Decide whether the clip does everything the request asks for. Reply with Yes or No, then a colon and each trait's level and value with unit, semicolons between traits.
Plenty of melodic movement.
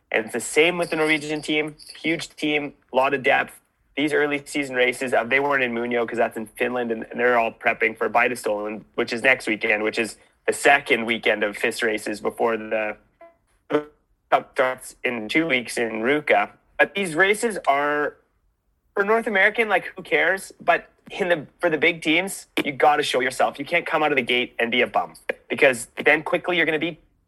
Yes: wide, 5.7 semitones